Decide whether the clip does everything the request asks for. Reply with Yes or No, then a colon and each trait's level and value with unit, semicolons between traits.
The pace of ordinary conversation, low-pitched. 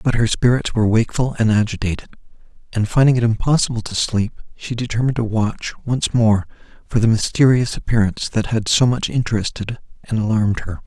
Yes: average, 170 wpm; low, 115 Hz